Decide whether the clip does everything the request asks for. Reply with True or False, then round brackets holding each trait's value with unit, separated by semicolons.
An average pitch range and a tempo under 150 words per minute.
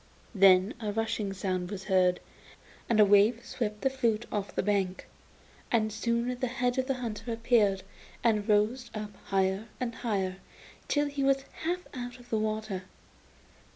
False (3.5 semitones; 160 wpm)